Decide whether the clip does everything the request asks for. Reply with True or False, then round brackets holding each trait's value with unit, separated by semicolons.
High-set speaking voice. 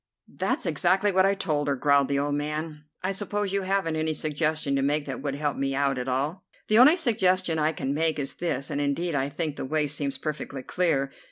False (150 Hz)